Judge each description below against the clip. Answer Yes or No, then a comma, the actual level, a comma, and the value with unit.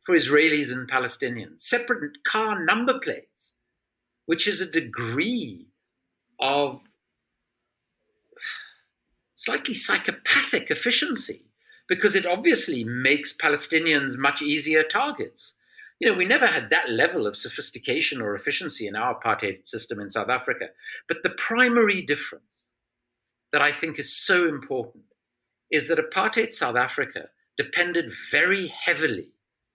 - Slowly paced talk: Yes, slow, 120 wpm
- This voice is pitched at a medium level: Yes, medium, 170 Hz